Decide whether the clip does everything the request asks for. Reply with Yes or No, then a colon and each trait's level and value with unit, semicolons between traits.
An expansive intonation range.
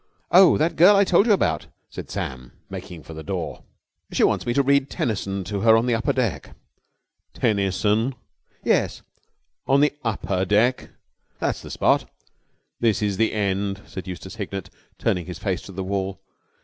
No: average, 4.6 semitones